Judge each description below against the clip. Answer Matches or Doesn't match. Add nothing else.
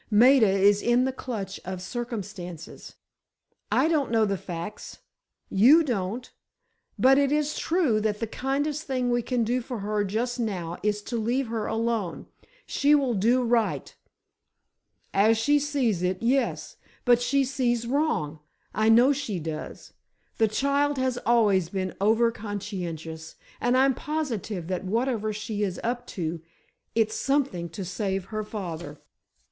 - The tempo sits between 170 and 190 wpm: Doesn't match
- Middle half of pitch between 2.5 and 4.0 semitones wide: Doesn't match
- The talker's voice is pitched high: Matches